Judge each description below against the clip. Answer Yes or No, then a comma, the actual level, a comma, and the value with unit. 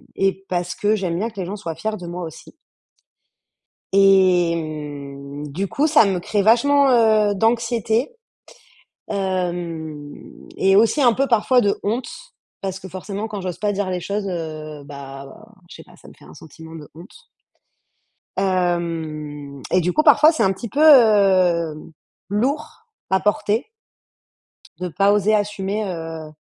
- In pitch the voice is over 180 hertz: Yes, high, 190 Hz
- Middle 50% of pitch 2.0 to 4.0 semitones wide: No, average, 4.4 semitones